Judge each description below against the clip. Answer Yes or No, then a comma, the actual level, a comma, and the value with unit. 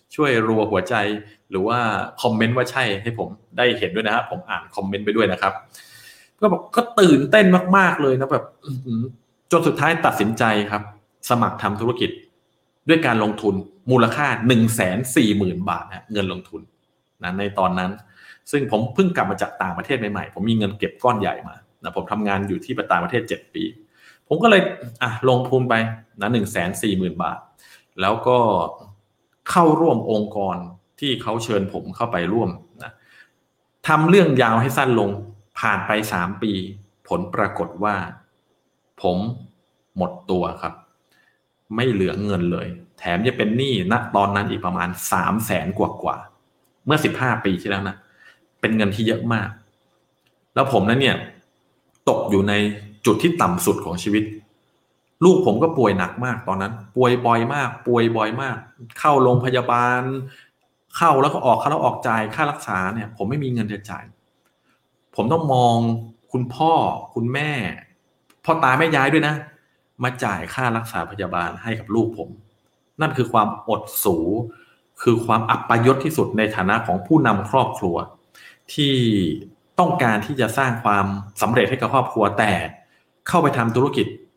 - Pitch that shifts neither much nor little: Yes, average, 4.0 semitones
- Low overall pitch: Yes, low, 115 Hz